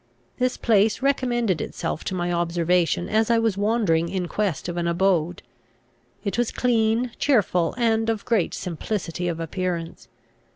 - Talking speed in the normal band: Yes, average, 150 wpm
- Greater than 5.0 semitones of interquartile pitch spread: No, average, 4.6 semitones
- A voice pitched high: Yes, high, 195 Hz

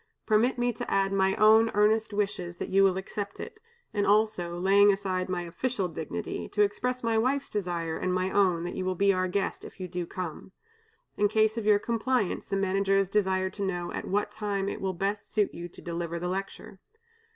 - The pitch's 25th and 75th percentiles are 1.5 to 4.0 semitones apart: Yes, narrow, 2.4 semitones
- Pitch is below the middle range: No, high, 195 Hz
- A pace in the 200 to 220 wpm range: Yes, fast, 205 wpm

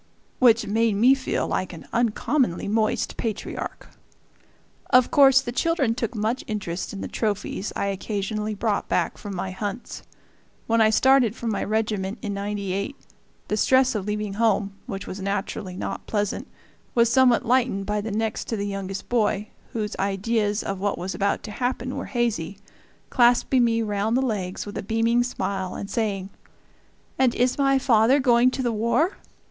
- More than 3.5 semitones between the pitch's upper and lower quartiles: No, average, 3.2 semitones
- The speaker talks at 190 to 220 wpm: No, average, 170 wpm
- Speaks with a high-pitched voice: Yes, high, 220 Hz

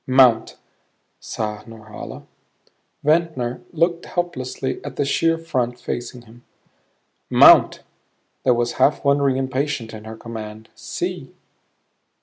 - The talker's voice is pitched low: Yes, low, 125 Hz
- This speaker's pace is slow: Yes, slow, 110 wpm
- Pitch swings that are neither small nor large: Yes, average, 4.1 semitones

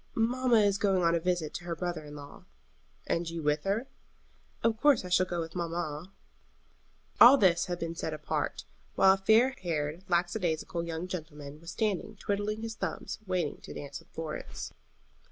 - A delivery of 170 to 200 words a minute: Yes, average, 175 wpm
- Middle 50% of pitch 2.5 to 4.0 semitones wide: Yes, average, 3.7 semitones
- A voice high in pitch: No, medium, 175 Hz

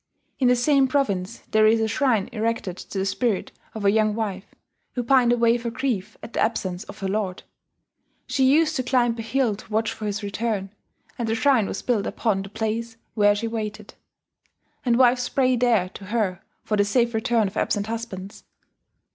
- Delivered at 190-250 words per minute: Yes, average, 195 wpm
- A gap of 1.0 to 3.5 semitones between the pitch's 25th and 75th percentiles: Yes, average, 2.9 semitones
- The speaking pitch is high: Yes, high, 225 Hz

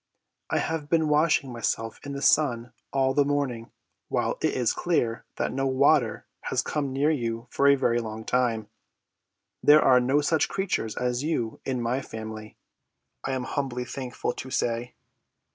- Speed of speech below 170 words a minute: Yes, average, 160 wpm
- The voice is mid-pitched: No, low, 130 Hz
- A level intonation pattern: No, average, 3.4 semitones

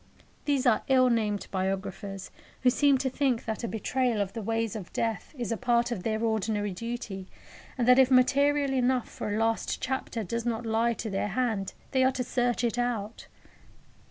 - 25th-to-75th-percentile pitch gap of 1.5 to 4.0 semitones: Yes, average, 2.8 semitones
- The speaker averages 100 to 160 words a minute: No, average, 190 wpm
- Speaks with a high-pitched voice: Yes, high, 230 Hz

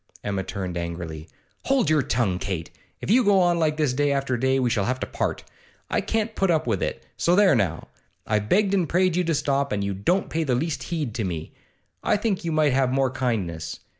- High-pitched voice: No, low, 135 Hz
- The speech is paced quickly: Yes, fast, 225 wpm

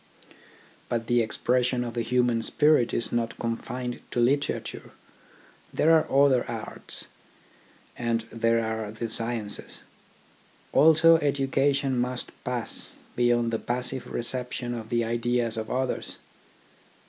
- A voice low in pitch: Yes, low, 120 Hz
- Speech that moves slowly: Yes, slow, 125 wpm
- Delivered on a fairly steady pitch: Yes, narrow, 1.8 semitones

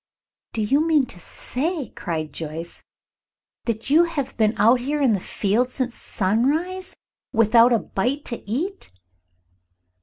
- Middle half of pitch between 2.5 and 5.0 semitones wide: No, wide, 5.5 semitones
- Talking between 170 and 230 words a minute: No, average, 140 wpm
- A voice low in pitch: No, high, 245 Hz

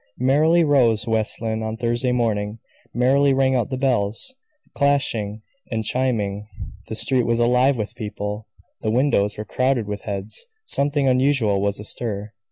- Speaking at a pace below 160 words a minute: Yes, average, 150 wpm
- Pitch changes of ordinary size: Yes, average, 3.9 semitones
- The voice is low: Yes, low, 115 Hz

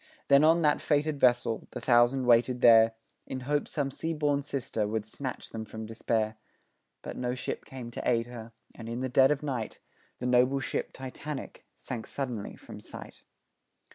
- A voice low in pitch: Yes, low, 125 Hz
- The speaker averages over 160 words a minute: Yes, average, 175 wpm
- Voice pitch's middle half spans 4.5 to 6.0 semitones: No, average, 3.1 semitones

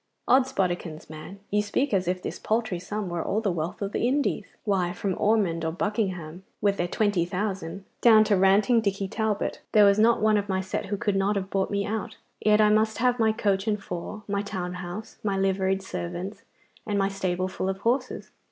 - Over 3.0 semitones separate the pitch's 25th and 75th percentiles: No, narrow, 2.5 semitones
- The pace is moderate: No, fast, 210 wpm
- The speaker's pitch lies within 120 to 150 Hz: No, high, 200 Hz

